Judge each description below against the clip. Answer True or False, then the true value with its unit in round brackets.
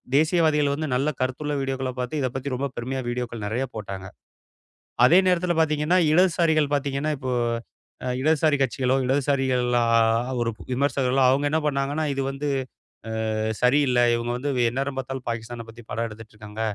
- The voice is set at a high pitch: False (135 Hz)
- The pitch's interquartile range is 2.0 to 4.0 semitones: True (3.1 semitones)